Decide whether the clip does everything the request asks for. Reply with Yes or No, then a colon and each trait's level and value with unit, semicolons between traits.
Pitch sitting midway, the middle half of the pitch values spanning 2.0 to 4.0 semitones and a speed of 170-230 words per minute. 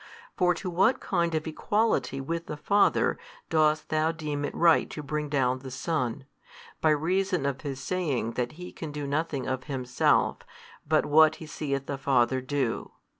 Yes: medium, 150 Hz; average, 3.4 semitones; average, 175 wpm